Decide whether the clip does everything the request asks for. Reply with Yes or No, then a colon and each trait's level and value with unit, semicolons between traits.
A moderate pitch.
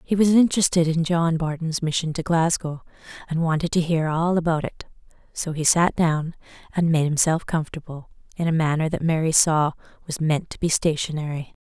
Yes: medium, 160 Hz